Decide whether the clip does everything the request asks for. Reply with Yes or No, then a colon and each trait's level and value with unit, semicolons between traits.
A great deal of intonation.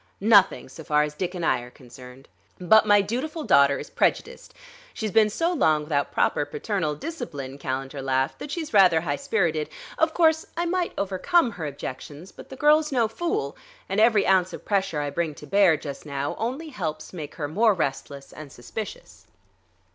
Yes: wide, 7.8 semitones